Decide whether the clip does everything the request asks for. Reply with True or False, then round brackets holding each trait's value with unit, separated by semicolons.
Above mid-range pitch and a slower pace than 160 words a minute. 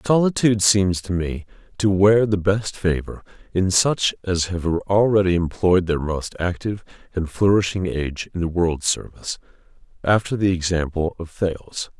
False (95 Hz; 150 wpm)